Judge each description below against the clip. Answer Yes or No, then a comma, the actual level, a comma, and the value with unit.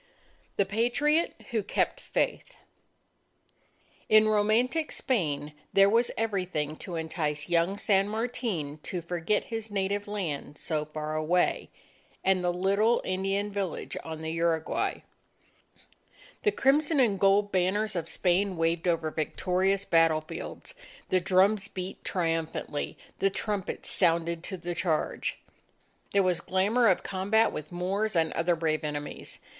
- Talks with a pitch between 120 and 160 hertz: No, medium, 185 Hz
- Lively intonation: No, average, 4.0 semitones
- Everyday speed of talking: No, slow, 130 wpm